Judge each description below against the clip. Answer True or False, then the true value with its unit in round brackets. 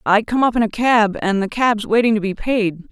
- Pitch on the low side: False (215 Hz)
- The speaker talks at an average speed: False (270 wpm)